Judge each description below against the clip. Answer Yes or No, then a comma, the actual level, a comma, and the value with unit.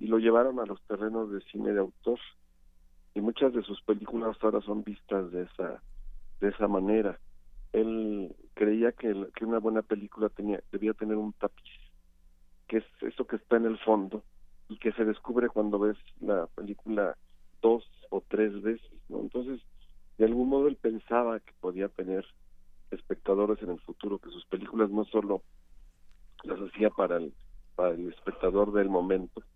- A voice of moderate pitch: No, low, 105 Hz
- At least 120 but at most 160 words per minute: No, average, 170 wpm